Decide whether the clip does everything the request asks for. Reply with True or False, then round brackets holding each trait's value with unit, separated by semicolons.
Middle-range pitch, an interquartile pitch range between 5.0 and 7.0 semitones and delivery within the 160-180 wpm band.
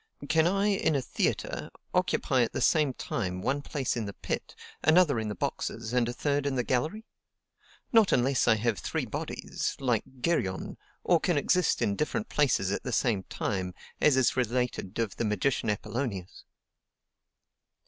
False (125 Hz; 5.6 semitones; 170 wpm)